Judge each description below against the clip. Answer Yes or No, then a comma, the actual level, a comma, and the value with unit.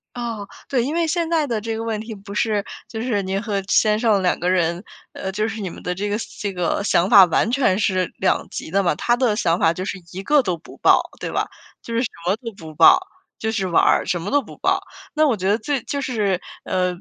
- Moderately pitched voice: No, high, 205 Hz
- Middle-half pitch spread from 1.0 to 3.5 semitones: No, average, 3.9 semitones